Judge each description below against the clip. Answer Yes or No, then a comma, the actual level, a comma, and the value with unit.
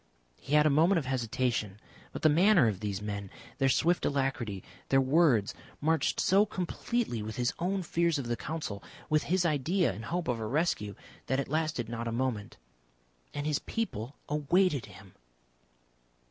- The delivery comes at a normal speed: Yes, average, 170 wpm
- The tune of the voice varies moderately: No, wide, 6.3 semitones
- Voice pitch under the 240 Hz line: Yes, medium, 140 Hz